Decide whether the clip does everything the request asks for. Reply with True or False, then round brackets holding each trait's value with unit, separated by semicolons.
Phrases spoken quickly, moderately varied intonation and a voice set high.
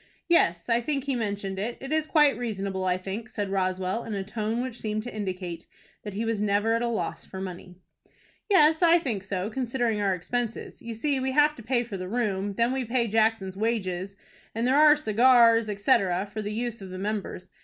True (210 wpm; 3.8 semitones; 220 Hz)